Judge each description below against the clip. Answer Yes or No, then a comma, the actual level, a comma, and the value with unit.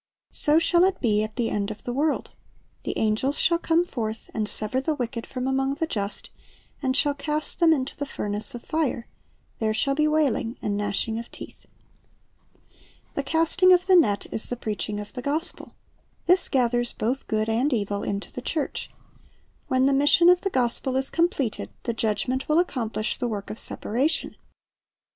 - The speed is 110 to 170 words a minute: No, average, 180 wpm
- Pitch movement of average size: No, wide, 5.7 semitones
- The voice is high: Yes, very high, 260 Hz